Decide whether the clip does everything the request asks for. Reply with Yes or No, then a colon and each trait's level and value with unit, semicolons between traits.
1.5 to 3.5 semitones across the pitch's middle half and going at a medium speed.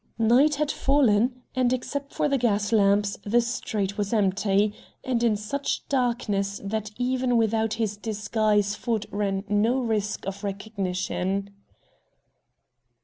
No: average, 3.2 semitones; slow, 130 wpm